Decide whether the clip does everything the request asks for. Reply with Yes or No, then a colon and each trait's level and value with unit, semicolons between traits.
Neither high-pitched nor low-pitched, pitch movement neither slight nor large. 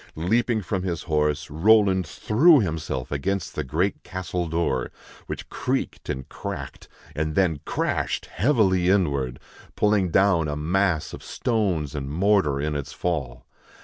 No: very low, 85 Hz; average, 4.6 semitones